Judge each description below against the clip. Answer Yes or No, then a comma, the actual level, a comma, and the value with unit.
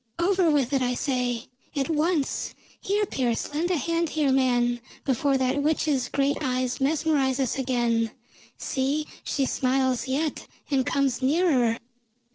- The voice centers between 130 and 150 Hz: No, very high, 270 Hz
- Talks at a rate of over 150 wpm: No, average, 140 wpm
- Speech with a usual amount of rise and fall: Yes, average, 3.1 semitones